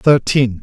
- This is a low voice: Yes, low, 125 Hz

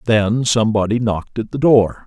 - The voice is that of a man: Yes, male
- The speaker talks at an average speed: Yes, average, 175 wpm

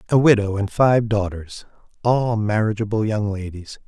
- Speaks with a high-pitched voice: No, low, 105 Hz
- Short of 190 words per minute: Yes, average, 140 wpm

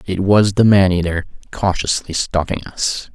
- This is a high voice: No, very low, 95 Hz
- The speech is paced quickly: No, average, 150 wpm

